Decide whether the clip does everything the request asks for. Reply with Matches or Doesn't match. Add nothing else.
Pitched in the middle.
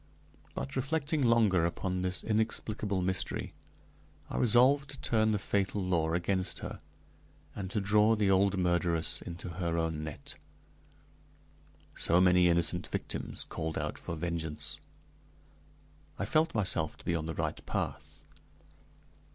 Doesn't match